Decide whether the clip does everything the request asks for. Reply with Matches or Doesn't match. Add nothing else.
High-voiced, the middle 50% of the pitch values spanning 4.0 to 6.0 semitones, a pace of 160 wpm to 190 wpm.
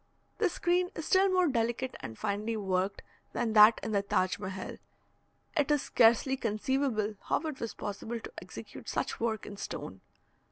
Matches